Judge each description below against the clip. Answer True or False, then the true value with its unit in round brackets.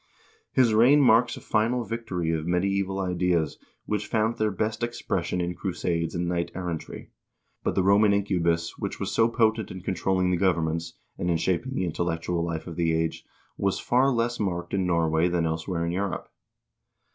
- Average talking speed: True (180 wpm)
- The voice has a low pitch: True (90 Hz)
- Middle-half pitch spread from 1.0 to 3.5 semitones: False (4.2 semitones)